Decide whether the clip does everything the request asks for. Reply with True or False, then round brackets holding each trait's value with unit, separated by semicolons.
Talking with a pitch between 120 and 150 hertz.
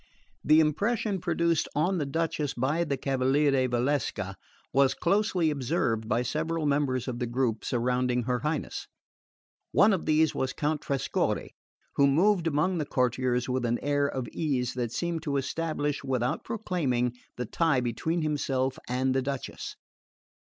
True (140 Hz)